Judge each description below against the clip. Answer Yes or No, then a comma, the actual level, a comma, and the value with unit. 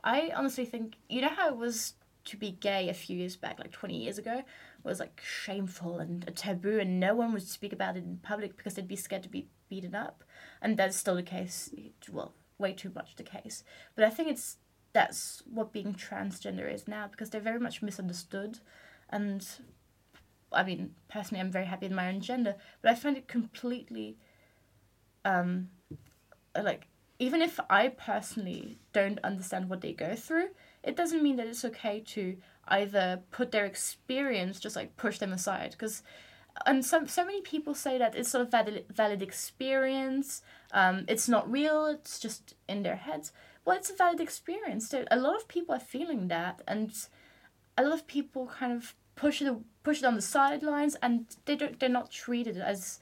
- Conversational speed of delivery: Yes, average, 190 wpm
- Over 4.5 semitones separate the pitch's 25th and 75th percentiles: Yes, wide, 5.6 semitones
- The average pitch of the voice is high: Yes, high, 220 Hz